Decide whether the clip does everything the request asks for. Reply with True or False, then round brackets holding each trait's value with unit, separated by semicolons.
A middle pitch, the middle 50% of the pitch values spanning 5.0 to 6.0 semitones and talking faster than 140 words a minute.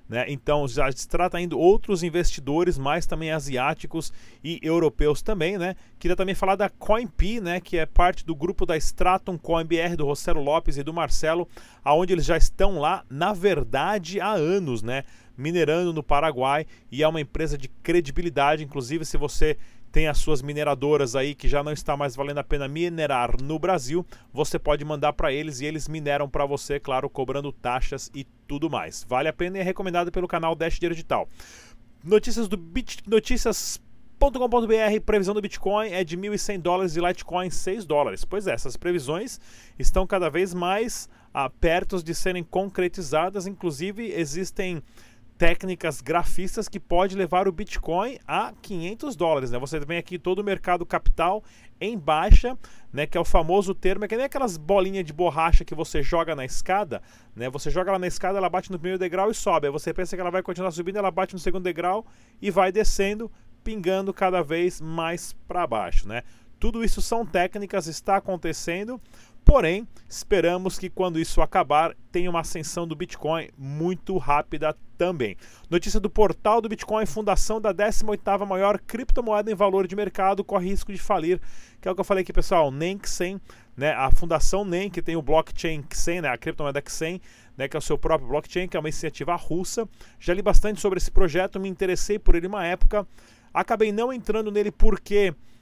False (175 Hz; 4.3 semitones; 185 wpm)